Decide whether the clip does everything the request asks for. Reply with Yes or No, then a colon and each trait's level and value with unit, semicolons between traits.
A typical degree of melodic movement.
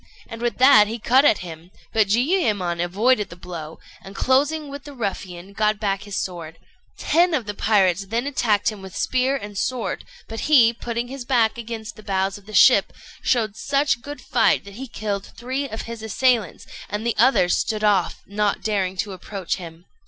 Yes: average, 4.2 semitones